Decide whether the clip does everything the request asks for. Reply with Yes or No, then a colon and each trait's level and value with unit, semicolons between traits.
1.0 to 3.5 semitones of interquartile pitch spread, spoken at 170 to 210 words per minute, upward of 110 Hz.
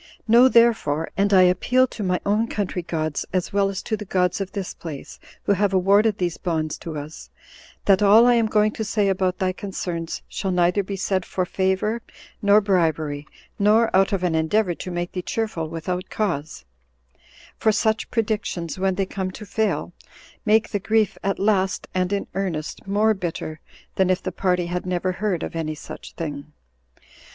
Yes: average, 3.1 semitones; average, 185 wpm; high, 190 Hz